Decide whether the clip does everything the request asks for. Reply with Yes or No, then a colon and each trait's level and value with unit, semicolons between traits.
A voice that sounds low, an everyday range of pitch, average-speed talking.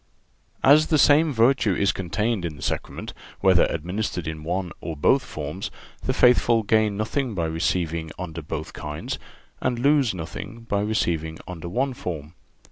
No: very low, 95 Hz; wide, 6.2 semitones; average, 160 wpm